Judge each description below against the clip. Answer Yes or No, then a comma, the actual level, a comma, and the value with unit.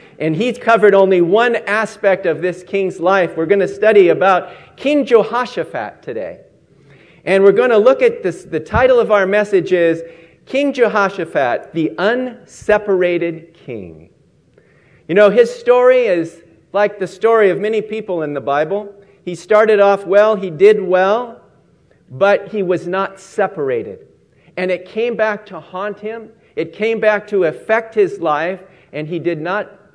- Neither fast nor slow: Yes, average, 160 wpm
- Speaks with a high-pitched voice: Yes, high, 200 Hz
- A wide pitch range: No, average, 3.9 semitones